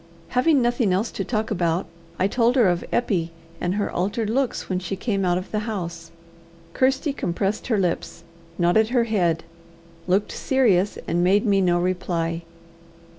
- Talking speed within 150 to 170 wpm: Yes, average, 165 wpm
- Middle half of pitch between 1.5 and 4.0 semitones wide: No, average, 4.6 semitones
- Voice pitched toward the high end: Yes, high, 195 Hz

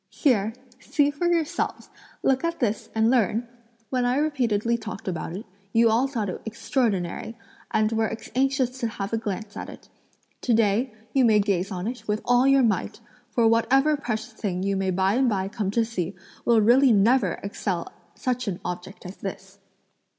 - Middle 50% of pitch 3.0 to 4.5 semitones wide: Yes, average, 4.0 semitones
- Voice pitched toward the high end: Yes, high, 225 Hz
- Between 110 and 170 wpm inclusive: No, average, 180 wpm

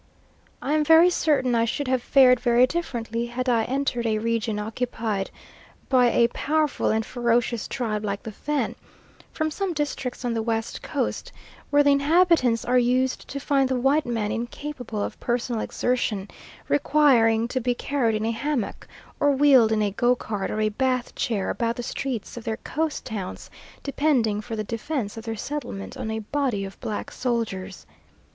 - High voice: Yes, high, 240 Hz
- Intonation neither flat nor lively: Yes, average, 3.7 semitones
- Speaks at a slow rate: No, average, 175 wpm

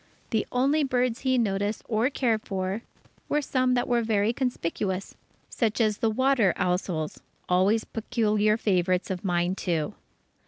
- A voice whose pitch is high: Yes, high, 215 Hz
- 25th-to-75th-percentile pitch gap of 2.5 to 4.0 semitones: No, average, 4.6 semitones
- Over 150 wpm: No, average, 145 wpm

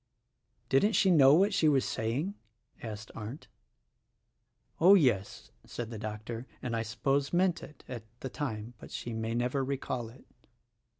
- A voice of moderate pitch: No, low, 125 Hz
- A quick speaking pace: No, average, 155 wpm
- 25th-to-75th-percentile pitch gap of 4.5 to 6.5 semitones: Yes, average, 4.8 semitones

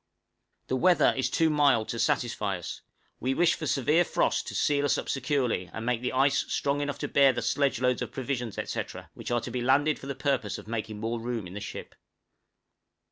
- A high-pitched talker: No, low, 130 Hz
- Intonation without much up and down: No, average, 3.5 semitones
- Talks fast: Yes, fast, 215 wpm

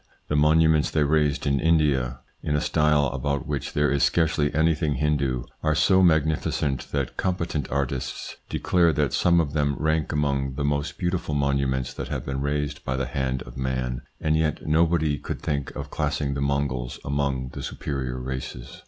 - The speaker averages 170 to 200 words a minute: Yes, average, 175 wpm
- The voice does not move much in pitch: Yes, narrow, 2.3 semitones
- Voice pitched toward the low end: Yes, very low, 70 Hz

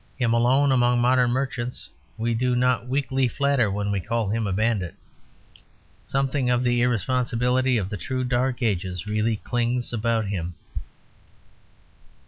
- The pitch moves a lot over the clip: No, average, 2.7 semitones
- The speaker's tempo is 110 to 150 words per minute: Yes, average, 140 wpm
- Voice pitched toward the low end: Yes, low, 120 Hz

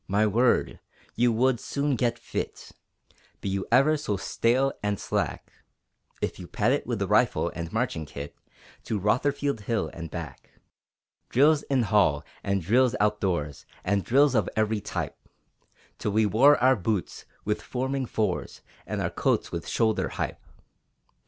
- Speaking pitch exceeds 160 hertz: No, low, 110 Hz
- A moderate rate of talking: Yes, average, 150 wpm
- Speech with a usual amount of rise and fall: Yes, average, 4.6 semitones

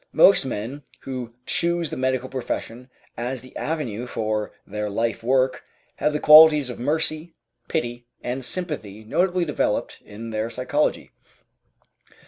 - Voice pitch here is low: Yes, low, 130 Hz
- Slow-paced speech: Yes, slow, 130 wpm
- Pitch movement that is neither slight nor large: Yes, average, 4.8 semitones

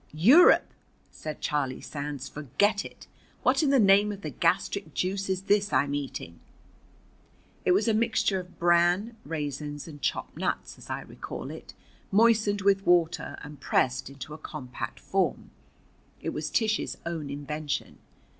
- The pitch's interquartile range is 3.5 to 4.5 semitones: No, wide, 5.6 semitones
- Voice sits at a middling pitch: Yes, medium, 170 Hz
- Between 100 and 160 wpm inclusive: Yes, average, 150 wpm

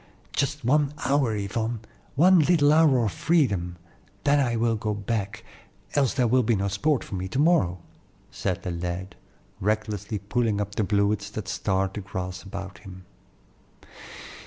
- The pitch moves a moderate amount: No, wide, 5.8 semitones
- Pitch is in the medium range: No, low, 105 Hz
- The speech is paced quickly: No, average, 160 wpm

